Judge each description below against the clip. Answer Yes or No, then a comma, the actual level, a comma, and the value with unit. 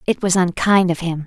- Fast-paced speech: Yes, fast, 240 wpm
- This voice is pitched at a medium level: Yes, medium, 180 Hz